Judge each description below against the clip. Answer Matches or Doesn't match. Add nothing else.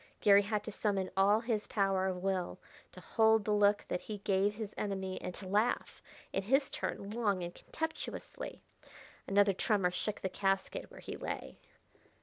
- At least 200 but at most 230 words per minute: Doesn't match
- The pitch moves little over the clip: Matches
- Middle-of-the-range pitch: Doesn't match